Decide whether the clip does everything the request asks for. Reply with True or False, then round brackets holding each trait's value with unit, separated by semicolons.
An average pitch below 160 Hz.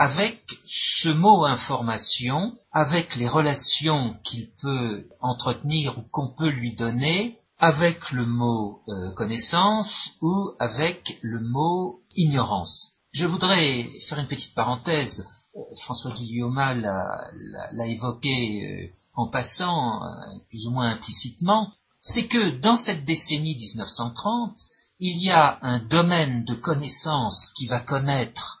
True (140 Hz)